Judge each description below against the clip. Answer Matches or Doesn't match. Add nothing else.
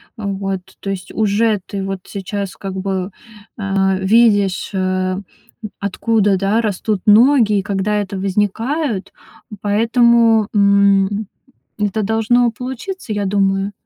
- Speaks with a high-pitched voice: Matches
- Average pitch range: Doesn't match